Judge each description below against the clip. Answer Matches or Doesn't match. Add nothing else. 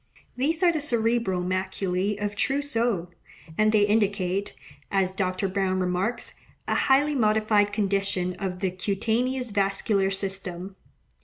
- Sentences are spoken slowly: Matches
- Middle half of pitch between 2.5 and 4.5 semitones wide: Matches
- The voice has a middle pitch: Doesn't match